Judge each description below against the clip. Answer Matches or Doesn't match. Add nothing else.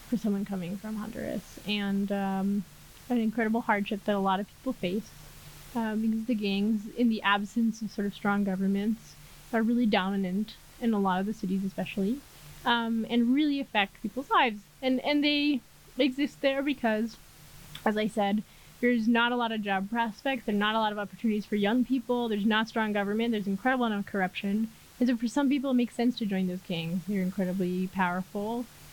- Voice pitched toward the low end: Doesn't match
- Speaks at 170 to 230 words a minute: Matches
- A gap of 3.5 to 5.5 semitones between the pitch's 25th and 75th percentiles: Doesn't match